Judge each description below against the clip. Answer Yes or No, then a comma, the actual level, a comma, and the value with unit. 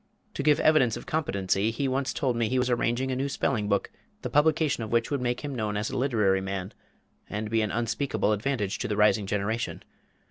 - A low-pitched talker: Yes, low, 115 Hz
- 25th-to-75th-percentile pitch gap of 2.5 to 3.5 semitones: No, average, 4.2 semitones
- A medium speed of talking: No, fast, 215 wpm